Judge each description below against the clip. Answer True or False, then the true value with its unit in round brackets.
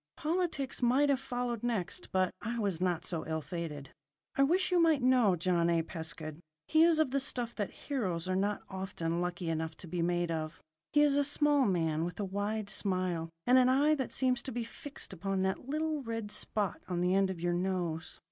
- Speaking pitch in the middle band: False (195 Hz)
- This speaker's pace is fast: True (210 wpm)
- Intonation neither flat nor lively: False (7.1 semitones)